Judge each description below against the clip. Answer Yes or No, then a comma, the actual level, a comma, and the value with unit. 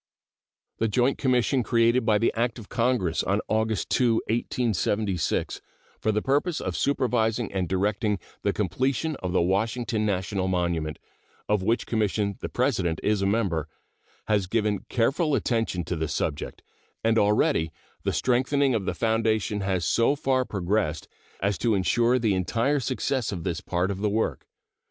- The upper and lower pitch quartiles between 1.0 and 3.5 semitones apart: No, average, 4.1 semitones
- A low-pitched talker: Yes, low, 110 Hz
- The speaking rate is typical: Yes, average, 155 wpm